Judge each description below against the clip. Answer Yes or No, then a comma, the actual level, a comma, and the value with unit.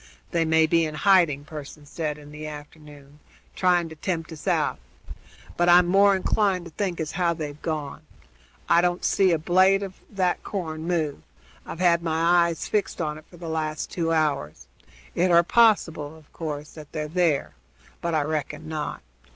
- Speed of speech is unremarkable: Yes, average, 180 wpm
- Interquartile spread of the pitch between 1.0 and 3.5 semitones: Yes, narrow, 2.5 semitones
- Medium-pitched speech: Yes, medium, 160 Hz